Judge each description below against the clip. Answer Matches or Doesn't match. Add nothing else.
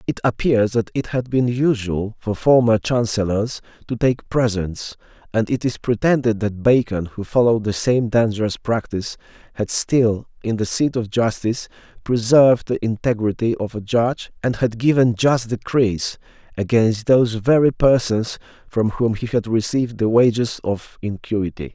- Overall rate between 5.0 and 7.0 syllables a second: Doesn't match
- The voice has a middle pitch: Doesn't match